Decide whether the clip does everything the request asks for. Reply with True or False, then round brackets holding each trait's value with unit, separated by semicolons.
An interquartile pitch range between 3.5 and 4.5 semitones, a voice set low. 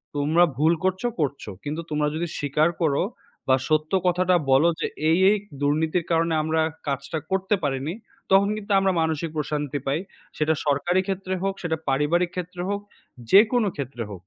False (3.8 semitones; 160 Hz)